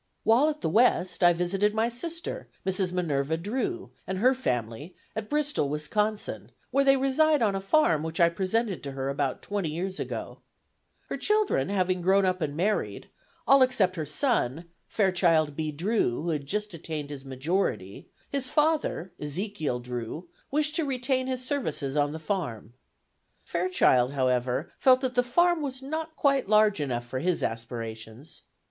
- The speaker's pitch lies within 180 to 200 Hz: Yes, medium, 185 Hz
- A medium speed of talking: Yes, average, 165 wpm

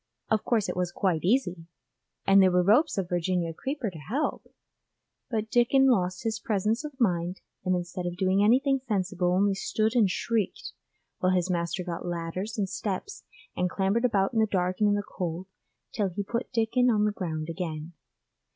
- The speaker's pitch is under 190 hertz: No, high, 195 Hz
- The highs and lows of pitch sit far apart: No, average, 3.8 semitones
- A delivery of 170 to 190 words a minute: Yes, average, 185 wpm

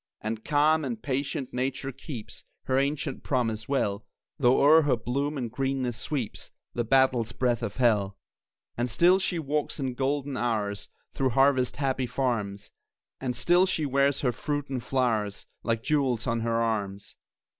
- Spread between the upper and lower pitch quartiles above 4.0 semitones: No, average, 3.3 semitones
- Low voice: Yes, low, 130 Hz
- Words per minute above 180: No, average, 155 wpm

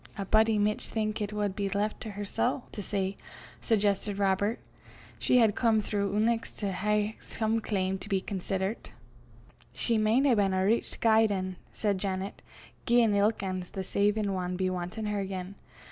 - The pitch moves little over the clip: Yes, narrow, 2.2 semitones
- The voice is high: Yes, high, 205 Hz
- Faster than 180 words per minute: No, average, 175 wpm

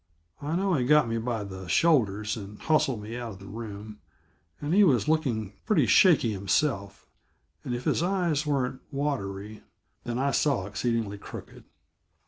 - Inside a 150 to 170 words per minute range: Yes, average, 160 wpm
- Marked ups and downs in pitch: Yes, wide, 6.3 semitones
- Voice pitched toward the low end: Yes, low, 120 Hz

